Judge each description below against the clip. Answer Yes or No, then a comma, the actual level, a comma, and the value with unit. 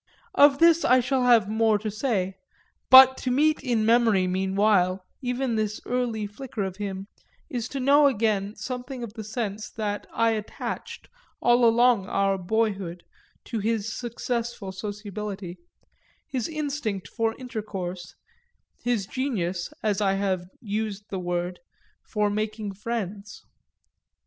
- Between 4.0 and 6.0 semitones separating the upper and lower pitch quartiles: No, average, 3.6 semitones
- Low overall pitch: No, high, 215 Hz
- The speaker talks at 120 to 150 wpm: Yes, slow, 135 wpm